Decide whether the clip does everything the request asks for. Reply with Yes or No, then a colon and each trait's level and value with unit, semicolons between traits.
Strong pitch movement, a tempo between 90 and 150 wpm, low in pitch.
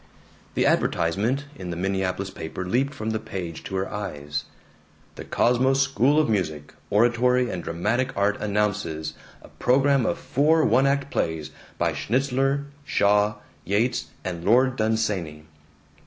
Yes: wide, 5.9 semitones; average, 140 wpm; low, 105 Hz